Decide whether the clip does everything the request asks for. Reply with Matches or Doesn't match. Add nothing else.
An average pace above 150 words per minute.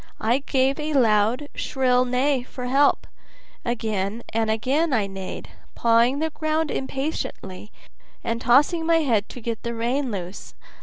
Doesn't match